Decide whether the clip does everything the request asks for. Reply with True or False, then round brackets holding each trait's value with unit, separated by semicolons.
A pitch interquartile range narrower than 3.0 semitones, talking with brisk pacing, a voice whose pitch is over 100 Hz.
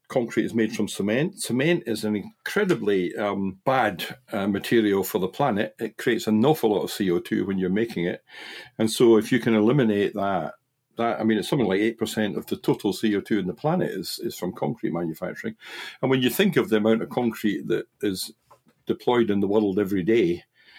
True (2.4 semitones; 210 wpm; 110 Hz)